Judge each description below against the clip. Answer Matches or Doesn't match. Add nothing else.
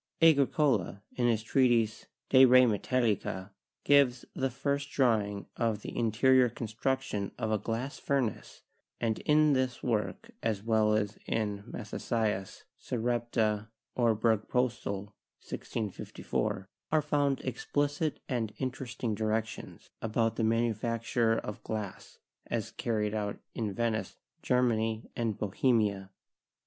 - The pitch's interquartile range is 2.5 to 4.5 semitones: Matches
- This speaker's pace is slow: Matches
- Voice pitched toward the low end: Matches